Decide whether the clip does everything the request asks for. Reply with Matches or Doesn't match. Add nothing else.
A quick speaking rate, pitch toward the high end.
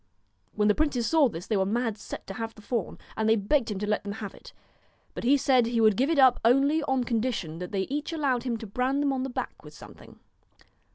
Matches